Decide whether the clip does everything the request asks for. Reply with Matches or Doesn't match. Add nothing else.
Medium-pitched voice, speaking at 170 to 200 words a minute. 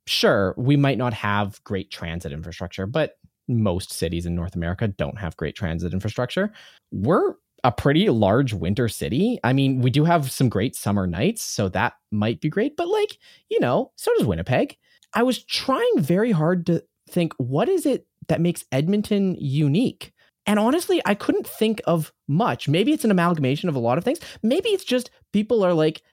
Matches